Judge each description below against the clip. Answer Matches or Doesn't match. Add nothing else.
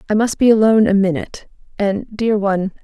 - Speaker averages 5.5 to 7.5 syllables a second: Matches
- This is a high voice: Matches